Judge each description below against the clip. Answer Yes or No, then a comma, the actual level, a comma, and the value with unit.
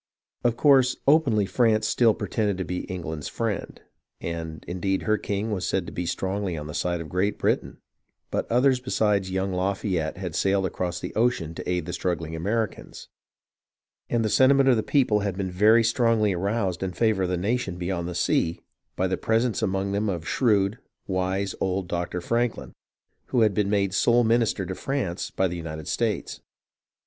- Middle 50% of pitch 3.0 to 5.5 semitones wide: Yes, average, 3.9 semitones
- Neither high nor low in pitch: No, low, 100 Hz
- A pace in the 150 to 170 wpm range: No, average, 180 wpm